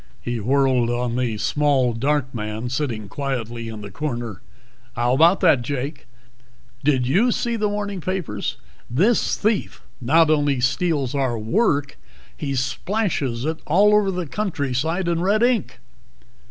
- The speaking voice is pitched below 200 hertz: Yes, medium, 140 Hz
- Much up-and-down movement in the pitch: Yes, wide, 6.6 semitones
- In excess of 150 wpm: No, average, 140 wpm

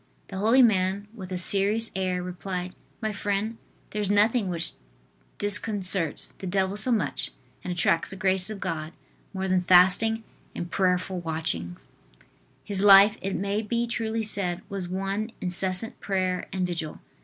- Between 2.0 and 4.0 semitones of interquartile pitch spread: Yes, narrow, 2.4 semitones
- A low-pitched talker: No, high, 190 Hz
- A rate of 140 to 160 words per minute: Yes, average, 155 wpm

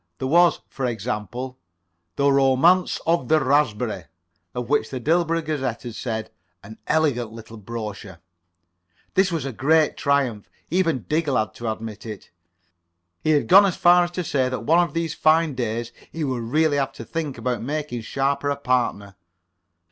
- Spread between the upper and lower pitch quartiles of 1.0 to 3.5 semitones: No, average, 5.1 semitones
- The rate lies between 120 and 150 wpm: No, average, 170 wpm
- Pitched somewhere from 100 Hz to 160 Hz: Yes, low, 135 Hz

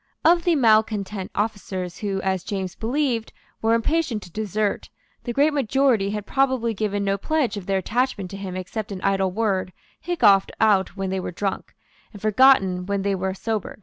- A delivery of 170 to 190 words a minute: Yes, average, 180 wpm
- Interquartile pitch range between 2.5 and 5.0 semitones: Yes, average, 3.3 semitones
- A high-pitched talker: Yes, high, 205 Hz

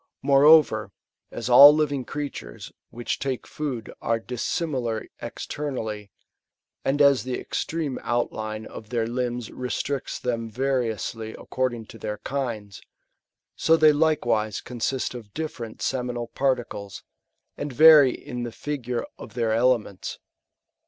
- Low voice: Yes, low, 125 Hz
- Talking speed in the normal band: No, slow, 125 wpm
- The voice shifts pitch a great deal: No, average, 3.7 semitones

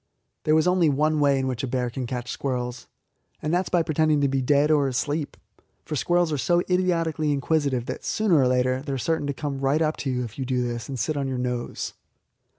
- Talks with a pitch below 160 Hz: Yes, medium, 140 Hz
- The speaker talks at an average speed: No, fast, 240 wpm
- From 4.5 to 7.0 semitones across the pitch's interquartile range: No, average, 3.5 semitones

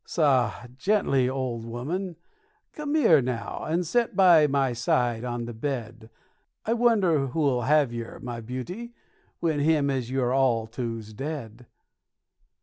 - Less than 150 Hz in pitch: Yes, low, 135 Hz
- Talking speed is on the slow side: No, average, 145 wpm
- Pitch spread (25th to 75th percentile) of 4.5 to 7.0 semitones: Yes, average, 5.2 semitones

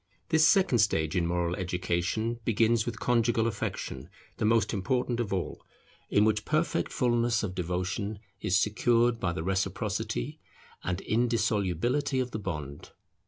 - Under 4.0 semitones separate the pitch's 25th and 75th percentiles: No, average, 4.5 semitones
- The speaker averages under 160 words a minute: Yes, average, 140 wpm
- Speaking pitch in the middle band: No, low, 110 Hz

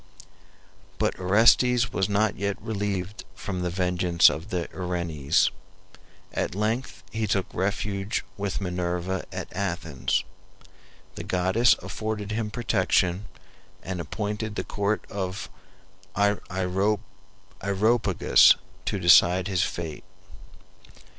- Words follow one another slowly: Yes, slow, 100 wpm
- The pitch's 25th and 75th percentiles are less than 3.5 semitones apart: Yes, average, 2.8 semitones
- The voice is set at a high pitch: No, very low, 95 Hz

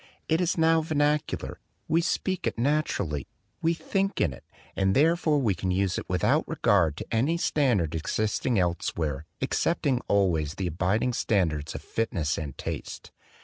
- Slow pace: No, average, 150 wpm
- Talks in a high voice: No, low, 105 Hz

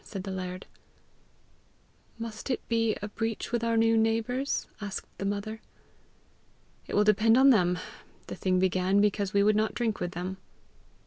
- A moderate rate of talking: Yes, average, 165 wpm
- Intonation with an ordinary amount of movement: Yes, average, 3.0 semitones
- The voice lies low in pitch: No, high, 215 Hz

